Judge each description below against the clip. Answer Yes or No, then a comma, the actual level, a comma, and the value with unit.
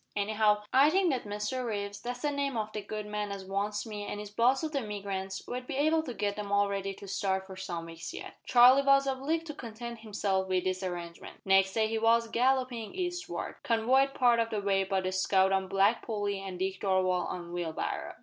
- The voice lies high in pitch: Yes, high, 210 Hz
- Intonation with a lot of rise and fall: No, average, 4.3 semitones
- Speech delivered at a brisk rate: Yes, fast, 220 wpm